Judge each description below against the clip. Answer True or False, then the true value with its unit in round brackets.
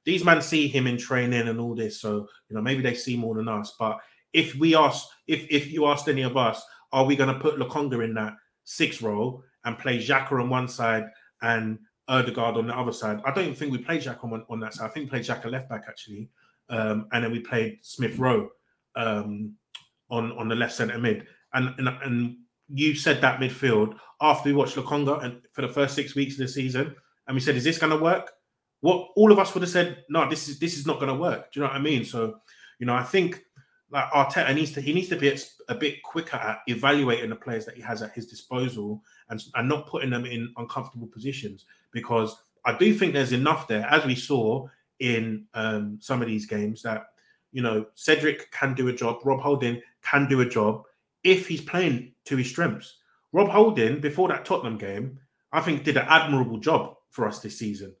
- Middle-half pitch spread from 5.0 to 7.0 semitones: False (4.2 semitones)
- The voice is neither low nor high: False (130 Hz)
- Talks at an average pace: False (225 wpm)